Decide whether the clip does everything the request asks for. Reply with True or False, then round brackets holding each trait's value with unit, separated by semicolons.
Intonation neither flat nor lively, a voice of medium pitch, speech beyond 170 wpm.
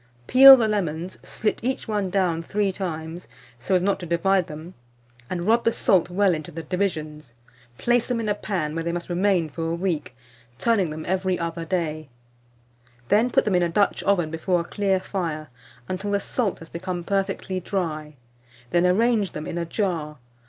True (3.5 semitones; 180 Hz; 190 wpm)